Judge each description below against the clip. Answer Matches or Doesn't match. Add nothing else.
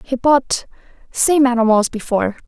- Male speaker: Doesn't match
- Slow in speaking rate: Matches